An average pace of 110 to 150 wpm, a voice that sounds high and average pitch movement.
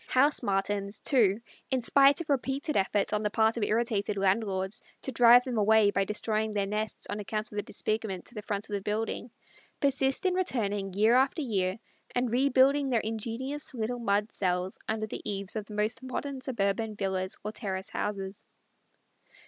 No: average, 180 wpm; high, 215 Hz; average, 3.8 semitones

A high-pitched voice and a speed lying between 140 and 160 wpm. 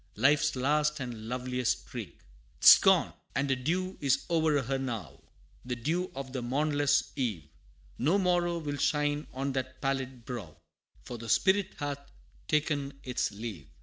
No: low, 135 Hz; average, 150 wpm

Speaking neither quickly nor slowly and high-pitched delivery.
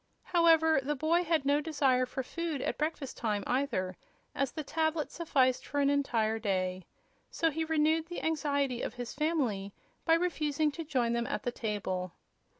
Yes: average, 170 wpm; very high, 285 Hz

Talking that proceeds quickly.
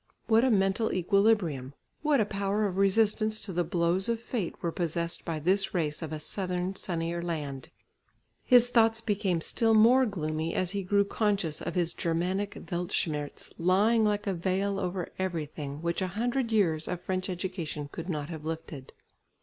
No: average, 170 wpm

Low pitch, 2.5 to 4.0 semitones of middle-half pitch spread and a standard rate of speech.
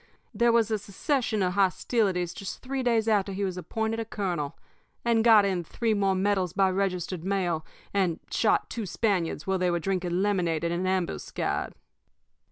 No: high, 195 Hz; average, 3.4 semitones; average, 175 wpm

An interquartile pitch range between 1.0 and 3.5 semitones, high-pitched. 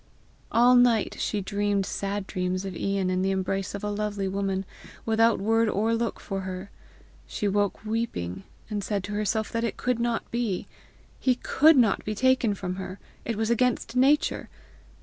Yes: average, 2.9 semitones; high, 205 Hz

